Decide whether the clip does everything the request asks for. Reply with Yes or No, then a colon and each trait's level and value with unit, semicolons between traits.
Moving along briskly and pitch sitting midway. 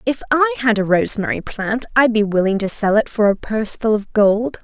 No: fast, 235 wpm; high, 215 Hz